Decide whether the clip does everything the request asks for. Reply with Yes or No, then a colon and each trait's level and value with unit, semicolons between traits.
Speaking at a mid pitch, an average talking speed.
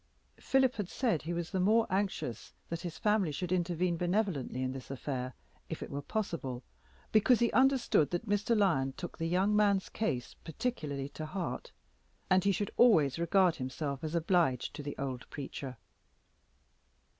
Yes: medium, 175 Hz; average, 165 wpm